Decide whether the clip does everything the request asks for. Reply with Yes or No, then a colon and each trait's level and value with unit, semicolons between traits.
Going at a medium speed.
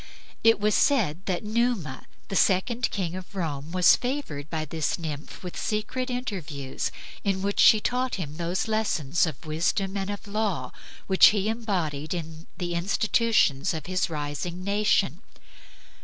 Yes: average, 150 wpm